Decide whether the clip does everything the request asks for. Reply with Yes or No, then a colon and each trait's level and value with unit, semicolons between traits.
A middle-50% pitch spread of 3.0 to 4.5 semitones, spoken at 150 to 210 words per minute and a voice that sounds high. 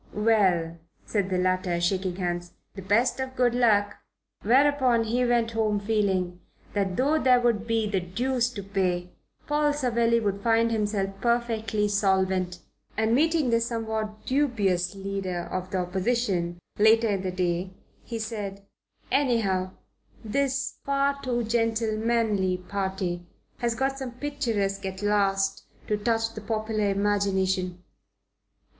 No: average, 3.7 semitones; slow, 135 wpm; high, 210 Hz